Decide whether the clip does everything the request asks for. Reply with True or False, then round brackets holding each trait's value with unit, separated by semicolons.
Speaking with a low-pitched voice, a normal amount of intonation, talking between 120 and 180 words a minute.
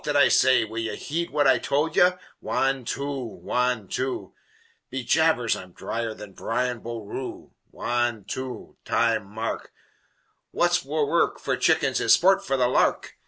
True (125 Hz; 3.8 semitones; 160 wpm)